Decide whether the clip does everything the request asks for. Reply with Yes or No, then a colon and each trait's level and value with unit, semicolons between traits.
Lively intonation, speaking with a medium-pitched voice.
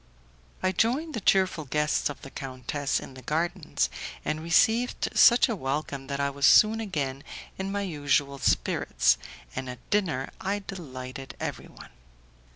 Yes: wide, 6.3 semitones; medium, 150 Hz